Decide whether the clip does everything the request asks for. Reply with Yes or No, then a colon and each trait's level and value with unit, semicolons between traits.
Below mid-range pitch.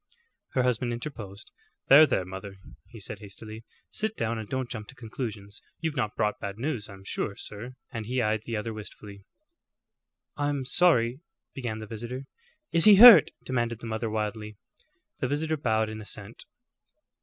Yes: low, 115 Hz